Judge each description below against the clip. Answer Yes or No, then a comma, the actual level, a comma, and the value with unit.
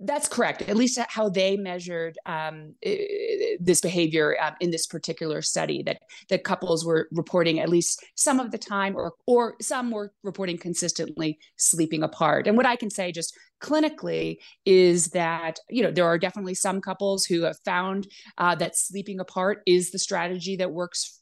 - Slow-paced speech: No, average, 175 wpm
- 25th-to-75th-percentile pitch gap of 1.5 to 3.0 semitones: No, average, 3.7 semitones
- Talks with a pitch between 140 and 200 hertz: Yes, medium, 185 Hz